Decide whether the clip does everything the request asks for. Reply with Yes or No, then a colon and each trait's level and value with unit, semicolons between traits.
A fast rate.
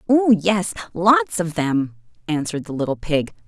No: average, 155 wpm